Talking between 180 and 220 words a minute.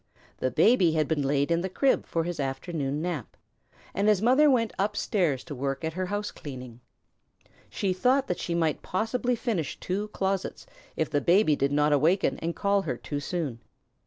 Yes: average, 190 wpm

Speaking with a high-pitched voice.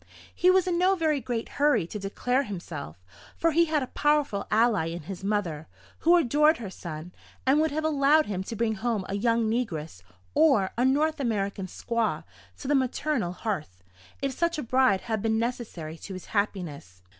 Yes: high, 230 Hz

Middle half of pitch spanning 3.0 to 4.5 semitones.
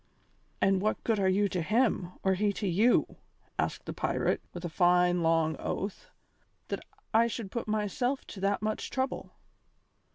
Yes: average, 3.4 semitones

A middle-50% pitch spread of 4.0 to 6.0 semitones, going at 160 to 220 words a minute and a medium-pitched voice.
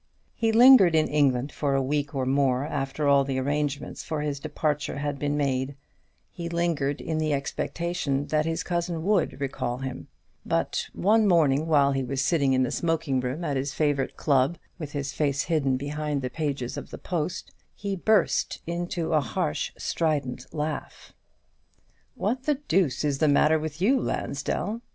No: average, 3.4 semitones; average, 170 wpm; medium, 150 Hz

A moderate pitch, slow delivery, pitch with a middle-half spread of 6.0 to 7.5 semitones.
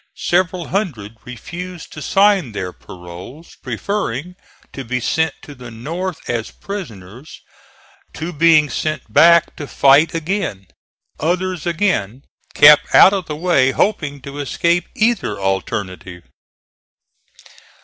Yes: medium, 150 Hz; slow, 120 wpm; wide, 6.8 semitones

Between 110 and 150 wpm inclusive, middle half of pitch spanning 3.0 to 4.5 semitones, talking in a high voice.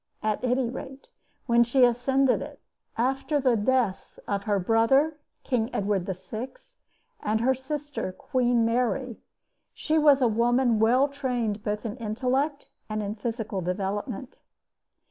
Yes: slow, 135 wpm; average, 3.6 semitones; high, 240 Hz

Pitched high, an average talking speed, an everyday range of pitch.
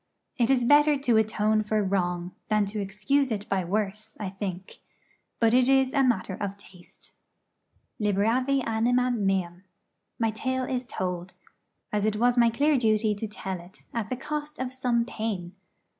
Yes: high, 220 Hz; average, 165 wpm; average, 4.1 semitones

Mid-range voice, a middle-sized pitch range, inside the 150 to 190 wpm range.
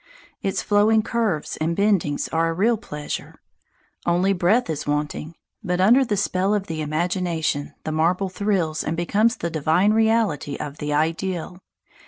Yes: medium, 180 Hz; average, 4.6 semitones; average, 155 wpm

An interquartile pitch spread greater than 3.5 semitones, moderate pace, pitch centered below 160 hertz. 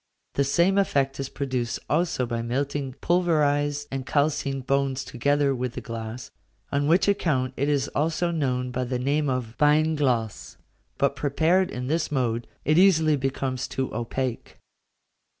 No: average, 3.1 semitones; average, 150 wpm; medium, 140 Hz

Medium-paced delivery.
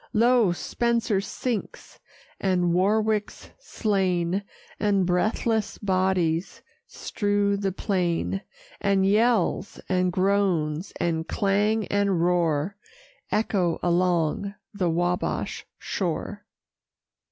No: slow, 85 wpm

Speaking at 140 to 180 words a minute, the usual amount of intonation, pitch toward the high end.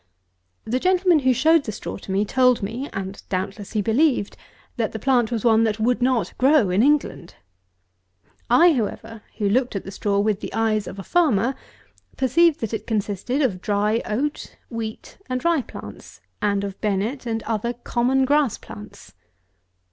Yes: average, 170 wpm; average, 4.3 semitones; high, 225 Hz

